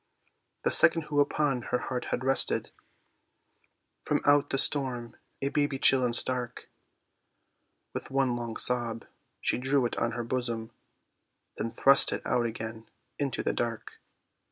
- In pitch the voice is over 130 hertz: No, low, 125 Hz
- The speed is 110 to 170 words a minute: Yes, average, 145 wpm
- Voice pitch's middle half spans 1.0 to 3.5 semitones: Yes, narrow, 2.6 semitones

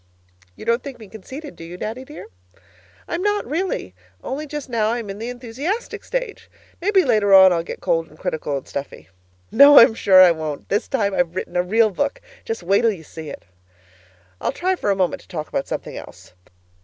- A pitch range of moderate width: No, wide, 7.9 semitones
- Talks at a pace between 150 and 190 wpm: No, fast, 205 wpm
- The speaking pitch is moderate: No, high, 220 Hz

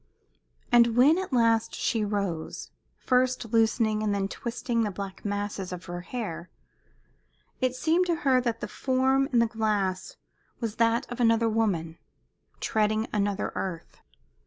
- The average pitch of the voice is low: No, high, 225 Hz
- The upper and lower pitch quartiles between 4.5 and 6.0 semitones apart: No, average, 3.3 semitones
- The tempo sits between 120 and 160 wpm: Yes, average, 145 wpm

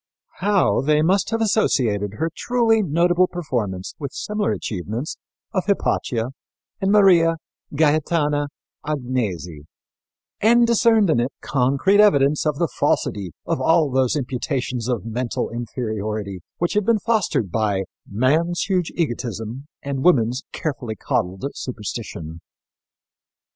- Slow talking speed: Yes, slow, 120 wpm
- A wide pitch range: Yes, wide, 7.6 semitones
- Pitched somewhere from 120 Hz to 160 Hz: Yes, medium, 140 Hz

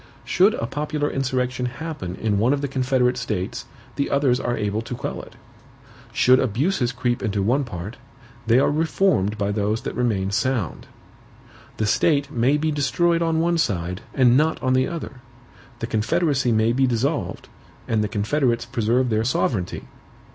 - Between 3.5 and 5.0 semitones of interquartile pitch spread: Yes, average, 4.6 semitones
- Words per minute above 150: Yes, average, 165 wpm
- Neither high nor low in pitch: No, low, 125 Hz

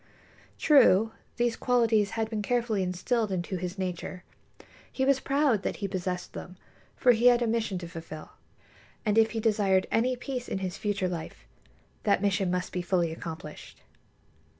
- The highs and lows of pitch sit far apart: No, average, 4.3 semitones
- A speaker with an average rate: Yes, average, 165 wpm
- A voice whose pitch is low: No, high, 205 Hz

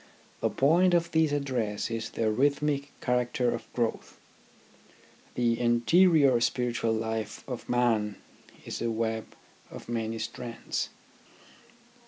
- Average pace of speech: No, slow, 115 wpm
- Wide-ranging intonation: No, average, 3.7 semitones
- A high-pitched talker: No, low, 120 Hz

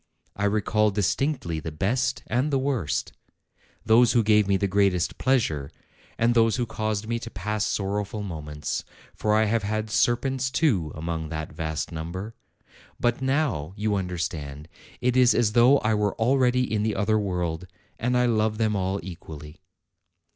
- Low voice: Yes, low, 105 Hz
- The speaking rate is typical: Yes, average, 165 wpm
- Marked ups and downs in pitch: No, average, 5.0 semitones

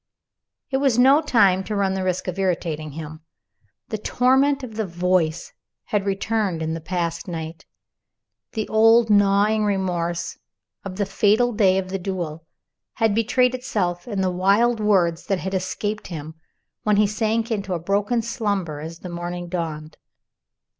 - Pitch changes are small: No, average, 4.0 semitones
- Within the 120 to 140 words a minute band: No, average, 160 wpm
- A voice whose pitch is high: Yes, high, 195 Hz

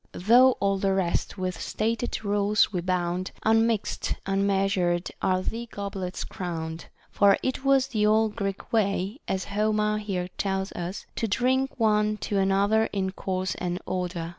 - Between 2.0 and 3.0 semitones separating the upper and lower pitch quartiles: Yes, average, 2.7 semitones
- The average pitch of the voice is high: Yes, high, 200 Hz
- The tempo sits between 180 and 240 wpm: No, average, 160 wpm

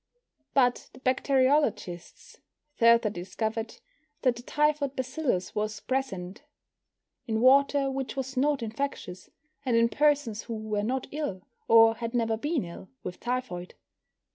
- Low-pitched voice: No, high, 240 Hz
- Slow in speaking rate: Yes, slow, 130 wpm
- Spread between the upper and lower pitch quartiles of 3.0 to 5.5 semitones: Yes, average, 3.9 semitones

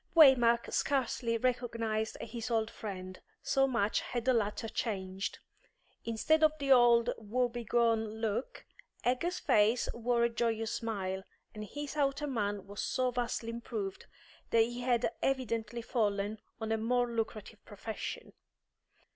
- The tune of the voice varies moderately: No, narrow, 2.3 semitones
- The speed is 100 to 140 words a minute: Yes, slow, 135 wpm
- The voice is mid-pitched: No, high, 230 Hz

